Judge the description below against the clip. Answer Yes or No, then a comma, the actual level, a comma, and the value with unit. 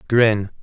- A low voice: Yes, low, 110 Hz